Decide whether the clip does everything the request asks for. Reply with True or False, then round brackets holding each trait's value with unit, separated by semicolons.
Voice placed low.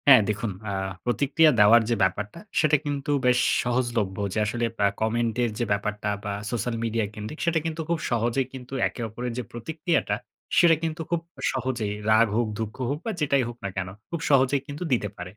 True (120 Hz)